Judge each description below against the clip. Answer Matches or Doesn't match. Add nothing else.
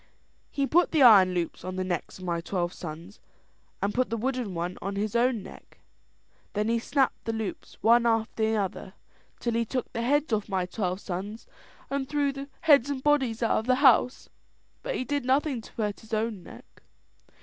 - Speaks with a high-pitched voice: Matches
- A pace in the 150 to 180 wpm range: Doesn't match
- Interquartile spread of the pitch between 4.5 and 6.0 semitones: Matches